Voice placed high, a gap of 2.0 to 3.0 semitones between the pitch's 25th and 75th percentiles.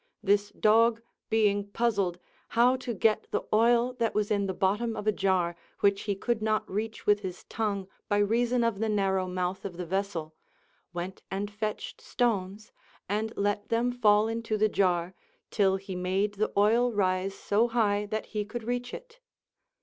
Yes: high, 205 Hz; narrow, 2.6 semitones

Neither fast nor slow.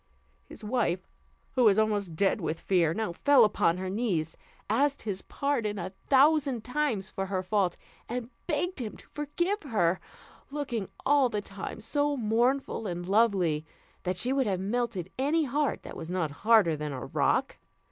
Yes: average, 170 wpm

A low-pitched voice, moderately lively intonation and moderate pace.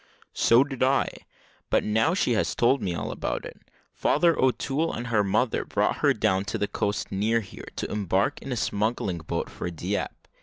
Yes: low, 110 Hz; average, 4.7 semitones; average, 190 wpm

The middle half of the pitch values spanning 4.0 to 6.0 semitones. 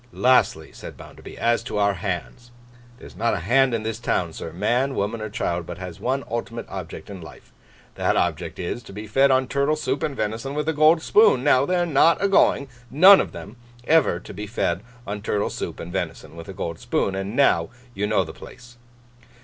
Yes: wide, 5.5 semitones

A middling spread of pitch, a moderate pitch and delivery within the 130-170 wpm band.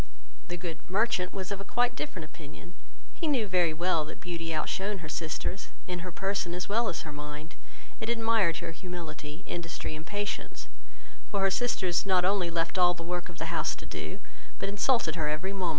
No: average, 3.2 semitones; medium, 180 Hz; fast, 205 wpm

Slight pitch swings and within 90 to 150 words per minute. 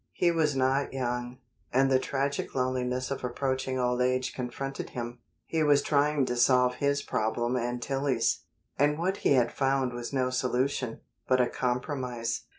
No: narrow, 1.9 semitones; average, 160 wpm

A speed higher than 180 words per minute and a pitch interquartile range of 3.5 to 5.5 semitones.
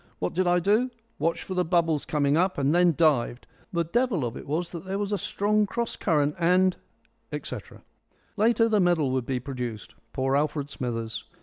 Yes: average, 195 wpm; average, 5.2 semitones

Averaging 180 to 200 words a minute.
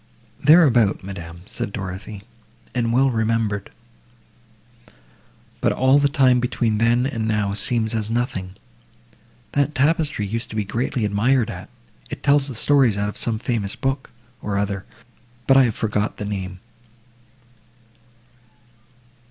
No: slow, 135 wpm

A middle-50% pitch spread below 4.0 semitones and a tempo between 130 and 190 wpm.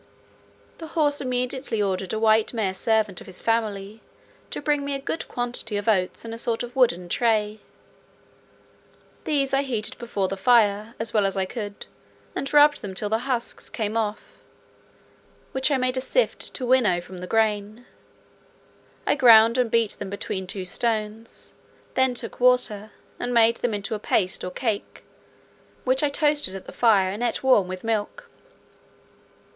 Yes: average, 3.6 semitones; average, 170 wpm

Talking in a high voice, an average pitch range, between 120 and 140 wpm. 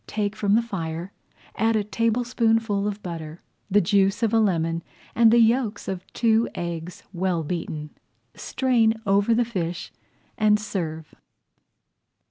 Yes: high, 205 Hz; average, 4.6 semitones; slow, 135 wpm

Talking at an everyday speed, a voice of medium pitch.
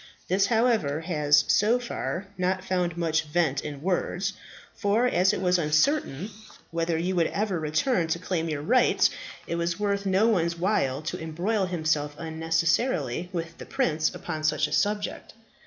Yes: average, 160 wpm; medium, 170 Hz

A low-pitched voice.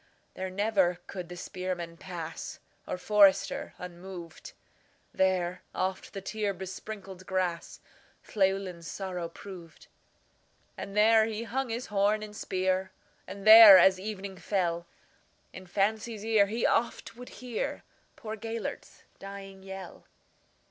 No: high, 195 Hz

